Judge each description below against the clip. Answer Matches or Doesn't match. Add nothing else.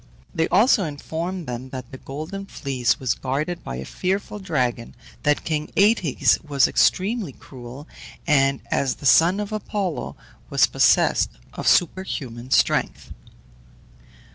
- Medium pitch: Matches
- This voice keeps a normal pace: Doesn't match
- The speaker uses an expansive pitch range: Matches